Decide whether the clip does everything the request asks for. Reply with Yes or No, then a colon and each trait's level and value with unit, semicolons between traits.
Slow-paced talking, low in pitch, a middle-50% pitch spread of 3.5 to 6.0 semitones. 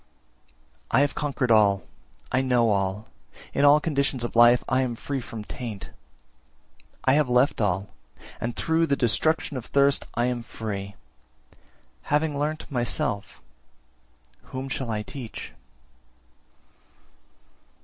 Yes: slow, 130 wpm; low, 125 Hz; average, 4.0 semitones